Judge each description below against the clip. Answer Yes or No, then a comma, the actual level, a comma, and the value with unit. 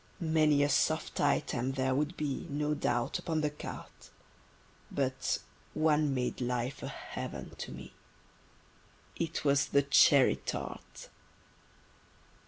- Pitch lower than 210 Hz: Yes, medium, 140 Hz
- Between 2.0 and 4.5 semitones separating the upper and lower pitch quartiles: Yes, narrow, 2.4 semitones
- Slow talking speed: Yes, slow, 120 wpm